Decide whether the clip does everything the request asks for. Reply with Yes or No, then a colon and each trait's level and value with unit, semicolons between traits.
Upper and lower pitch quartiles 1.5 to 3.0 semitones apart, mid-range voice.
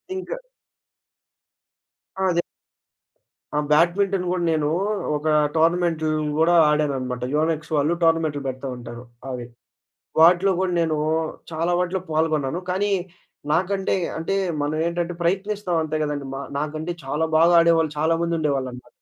Yes: average, 2.7 semitones; medium, 160 Hz